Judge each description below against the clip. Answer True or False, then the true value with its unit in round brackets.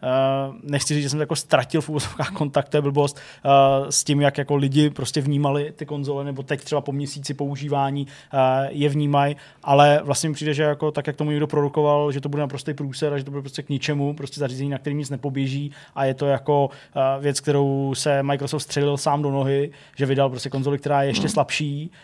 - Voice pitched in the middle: True (145 Hz)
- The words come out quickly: True (220 wpm)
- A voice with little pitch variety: True (1.1 semitones)